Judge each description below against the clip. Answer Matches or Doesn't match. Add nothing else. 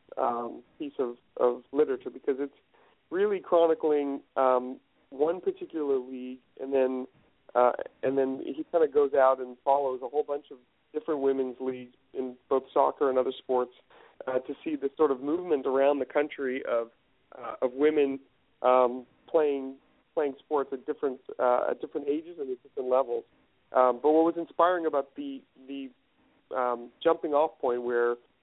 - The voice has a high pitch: Doesn't match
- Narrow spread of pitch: Doesn't match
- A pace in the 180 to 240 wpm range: Doesn't match